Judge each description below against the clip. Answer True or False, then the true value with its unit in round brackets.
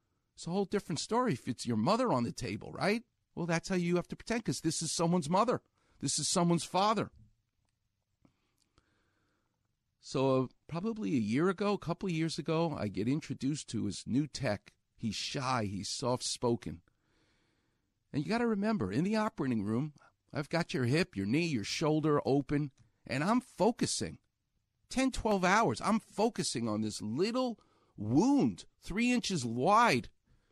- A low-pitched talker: False (155 Hz)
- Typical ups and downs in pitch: False (8.6 semitones)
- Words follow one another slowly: False (165 wpm)